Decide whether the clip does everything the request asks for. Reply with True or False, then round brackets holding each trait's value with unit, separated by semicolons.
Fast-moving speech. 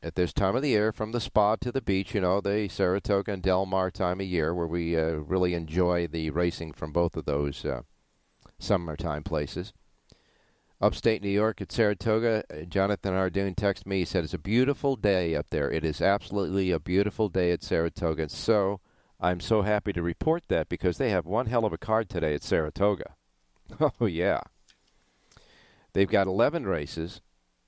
False (185 wpm)